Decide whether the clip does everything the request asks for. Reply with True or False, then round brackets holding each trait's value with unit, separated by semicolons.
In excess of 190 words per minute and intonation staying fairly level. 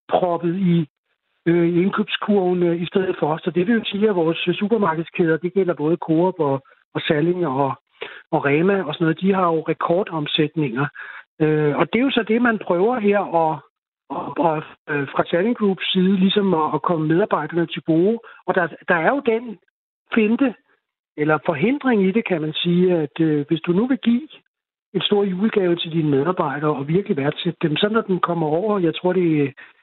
False (200 wpm; 3.9 semitones)